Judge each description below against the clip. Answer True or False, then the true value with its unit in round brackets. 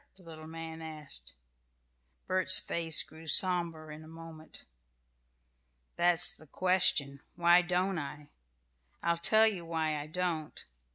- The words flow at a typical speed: False (125 wpm)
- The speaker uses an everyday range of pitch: False (2.2 semitones)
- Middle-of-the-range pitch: True (165 Hz)